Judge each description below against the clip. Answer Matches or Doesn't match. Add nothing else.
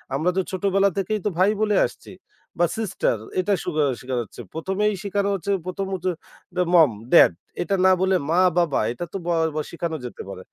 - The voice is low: Doesn't match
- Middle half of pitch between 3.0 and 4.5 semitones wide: Matches